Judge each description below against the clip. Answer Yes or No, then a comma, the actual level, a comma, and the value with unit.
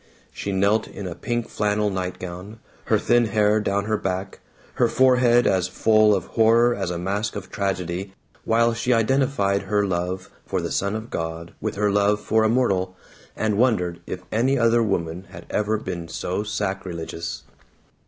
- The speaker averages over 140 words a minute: Yes, average, 170 wpm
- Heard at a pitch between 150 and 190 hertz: No, low, 100 Hz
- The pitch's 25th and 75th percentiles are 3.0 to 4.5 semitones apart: Yes, average, 3.3 semitones